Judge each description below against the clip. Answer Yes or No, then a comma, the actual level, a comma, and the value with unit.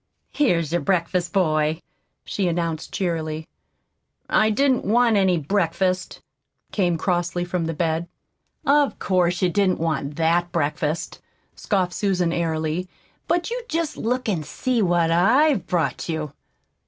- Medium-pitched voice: Yes, medium, 175 Hz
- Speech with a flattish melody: No, average, 3.6 semitones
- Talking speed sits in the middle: No, slow, 130 wpm